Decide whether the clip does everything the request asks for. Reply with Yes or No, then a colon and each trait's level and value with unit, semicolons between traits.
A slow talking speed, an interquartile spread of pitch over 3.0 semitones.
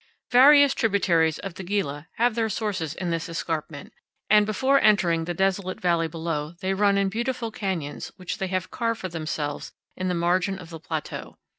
No: average, 180 wpm; average, 4.0 semitones